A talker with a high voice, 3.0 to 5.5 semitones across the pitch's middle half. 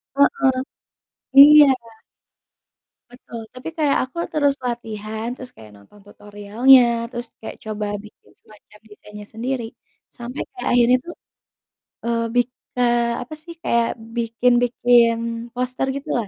No: high, 240 Hz; narrow, 2.5 semitones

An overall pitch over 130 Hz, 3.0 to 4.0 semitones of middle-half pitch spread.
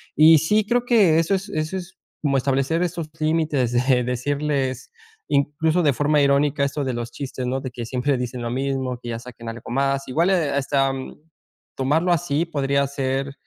Yes: medium, 140 Hz; average, 3.3 semitones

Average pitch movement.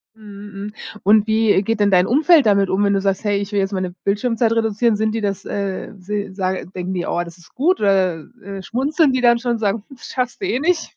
Yes: average, 3.1 semitones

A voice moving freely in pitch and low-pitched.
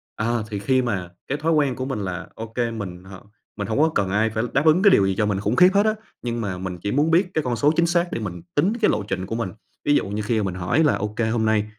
Yes: wide, 6.6 semitones; low, 110 Hz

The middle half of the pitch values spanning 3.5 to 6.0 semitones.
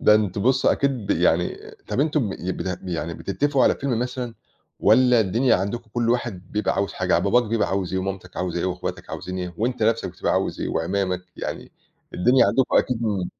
Yes: average, 5.0 semitones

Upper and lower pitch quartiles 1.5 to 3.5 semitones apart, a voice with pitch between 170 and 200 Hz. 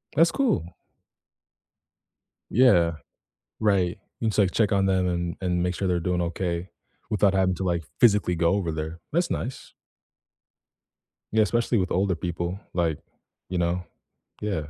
No: average, 2.8 semitones; very low, 90 Hz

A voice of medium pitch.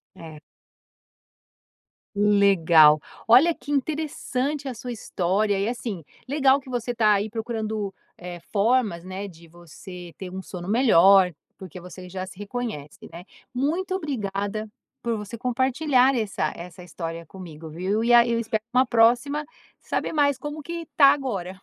No: high, 215 Hz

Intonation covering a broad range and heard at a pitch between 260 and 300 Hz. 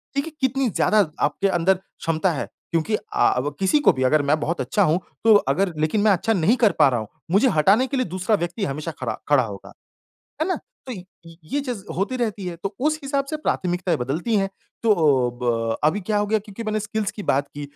No: wide, 6.0 semitones; high, 195 Hz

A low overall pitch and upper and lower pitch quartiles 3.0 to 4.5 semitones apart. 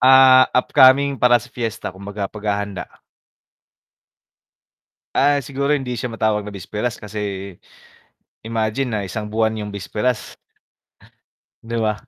Yes: low, 110 Hz; average, 3.5 semitones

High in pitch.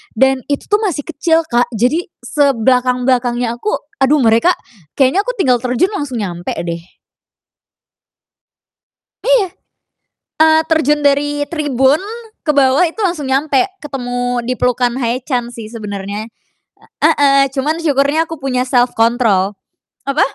Yes: very high, 265 Hz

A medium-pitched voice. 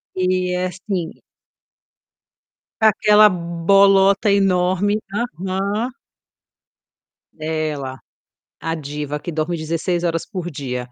Yes: medium, 180 Hz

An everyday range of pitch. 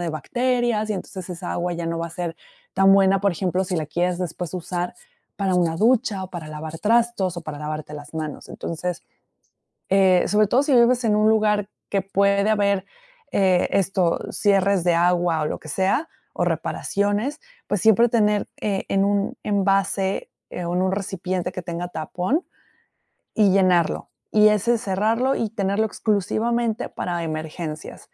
Yes: average, 3.2 semitones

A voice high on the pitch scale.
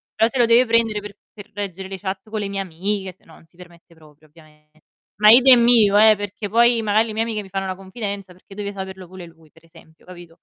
Yes: high, 195 Hz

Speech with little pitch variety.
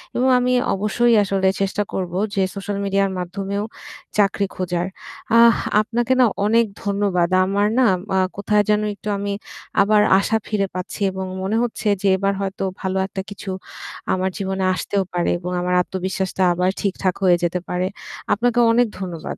Yes: narrow, 2.0 semitones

